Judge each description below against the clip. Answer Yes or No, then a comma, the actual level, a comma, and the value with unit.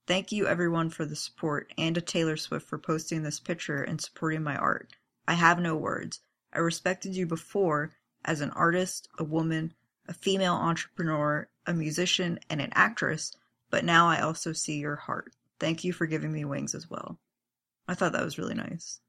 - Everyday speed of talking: Yes, average, 190 wpm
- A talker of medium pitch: Yes, medium, 165 Hz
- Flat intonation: Yes, narrow, 2.0 semitones